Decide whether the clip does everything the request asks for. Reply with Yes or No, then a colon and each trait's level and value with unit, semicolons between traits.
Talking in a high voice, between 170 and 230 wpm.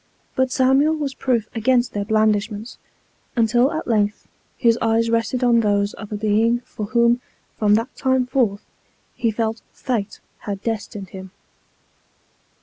No: high, 230 Hz; average, 145 wpm